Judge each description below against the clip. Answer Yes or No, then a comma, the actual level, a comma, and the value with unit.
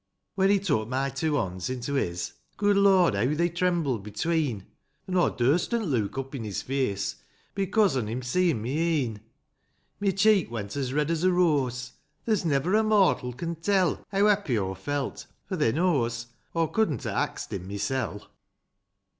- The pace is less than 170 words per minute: No, average, 180 wpm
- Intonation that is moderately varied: No, wide, 7.4 semitones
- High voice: No, medium, 145 Hz